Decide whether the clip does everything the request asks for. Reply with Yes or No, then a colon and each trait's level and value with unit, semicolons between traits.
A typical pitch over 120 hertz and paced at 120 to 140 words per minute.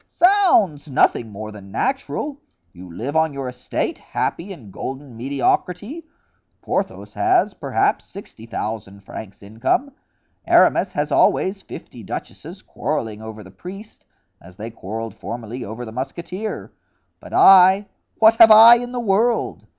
Yes: medium, 140 Hz; slow, 135 wpm